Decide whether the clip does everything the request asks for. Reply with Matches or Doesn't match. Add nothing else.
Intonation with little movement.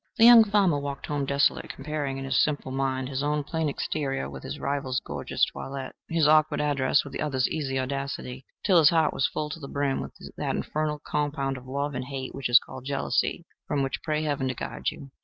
Matches